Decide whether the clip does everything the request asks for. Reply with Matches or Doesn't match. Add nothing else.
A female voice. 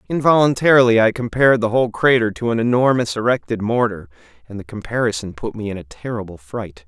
Doesn't match